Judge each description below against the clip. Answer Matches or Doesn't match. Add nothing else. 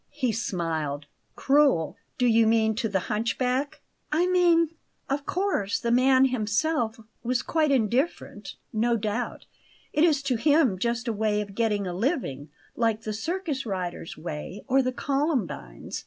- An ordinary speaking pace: Matches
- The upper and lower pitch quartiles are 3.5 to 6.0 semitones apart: Matches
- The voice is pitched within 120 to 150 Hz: Doesn't match